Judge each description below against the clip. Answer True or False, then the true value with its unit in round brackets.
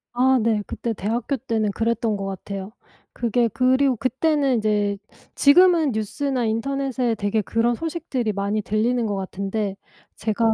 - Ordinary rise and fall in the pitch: True (3.6 semitones)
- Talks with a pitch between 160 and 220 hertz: False (230 Hz)